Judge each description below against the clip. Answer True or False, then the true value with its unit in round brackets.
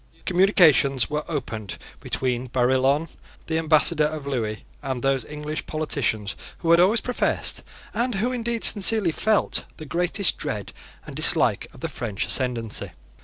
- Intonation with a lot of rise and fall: True (5.8 semitones)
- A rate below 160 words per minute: True (140 wpm)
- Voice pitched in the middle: True (150 Hz)